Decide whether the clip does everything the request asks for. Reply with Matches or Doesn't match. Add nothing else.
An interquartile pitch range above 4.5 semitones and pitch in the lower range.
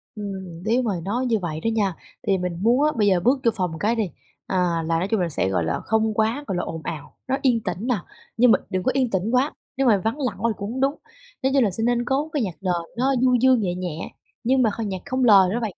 Doesn't match